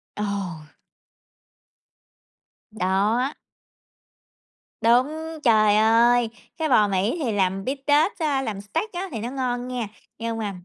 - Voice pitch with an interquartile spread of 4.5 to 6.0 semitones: No, average, 4.0 semitones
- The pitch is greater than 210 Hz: Yes, high, 230 Hz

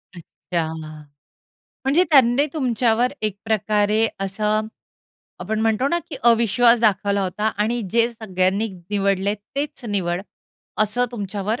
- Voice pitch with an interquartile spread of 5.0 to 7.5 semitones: No, average, 3.1 semitones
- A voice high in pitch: Yes, high, 215 Hz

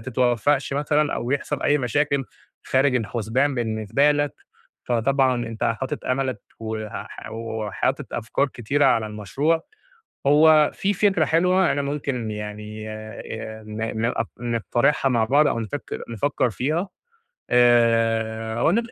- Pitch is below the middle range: Yes, low, 125 Hz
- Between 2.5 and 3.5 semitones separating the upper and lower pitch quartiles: No, average, 4.5 semitones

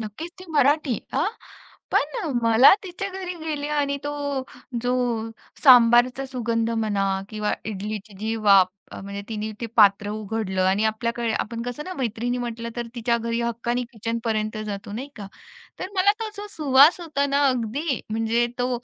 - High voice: Yes, high, 235 Hz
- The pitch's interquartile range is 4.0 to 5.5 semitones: Yes, average, 4.4 semitones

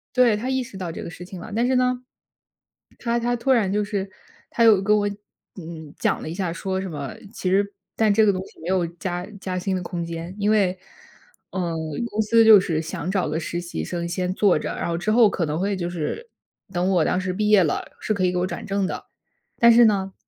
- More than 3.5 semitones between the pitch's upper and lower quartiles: No, average, 3.2 semitones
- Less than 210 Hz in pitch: Yes, high, 190 Hz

